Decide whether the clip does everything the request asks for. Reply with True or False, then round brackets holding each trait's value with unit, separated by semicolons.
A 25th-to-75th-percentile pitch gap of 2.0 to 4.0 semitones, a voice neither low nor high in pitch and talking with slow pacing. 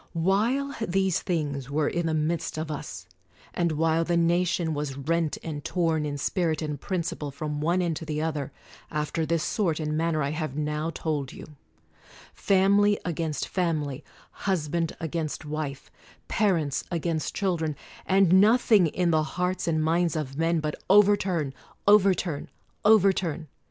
False (2.9 semitones; 165 Hz; 155 wpm)